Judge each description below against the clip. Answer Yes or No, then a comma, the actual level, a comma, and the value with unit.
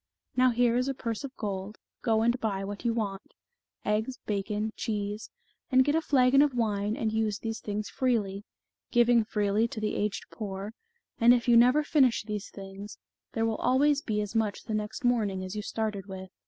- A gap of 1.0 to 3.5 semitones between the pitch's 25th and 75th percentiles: Yes, average, 2.9 semitones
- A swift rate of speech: No, average, 195 wpm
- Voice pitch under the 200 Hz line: No, high, 220 Hz